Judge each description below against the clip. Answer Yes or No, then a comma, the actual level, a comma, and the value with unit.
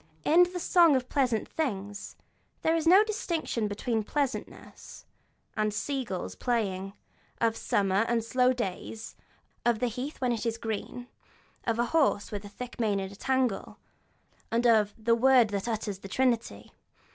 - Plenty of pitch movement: No, average, 3.9 semitones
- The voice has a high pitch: Yes, high, 235 Hz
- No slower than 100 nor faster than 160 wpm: No, average, 170 wpm